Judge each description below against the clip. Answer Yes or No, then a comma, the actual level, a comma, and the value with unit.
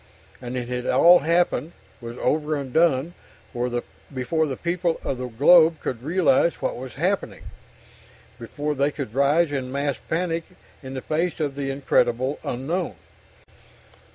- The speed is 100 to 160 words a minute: Yes, average, 145 wpm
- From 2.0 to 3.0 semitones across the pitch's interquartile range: No, average, 4.1 semitones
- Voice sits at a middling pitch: Yes, medium, 145 Hz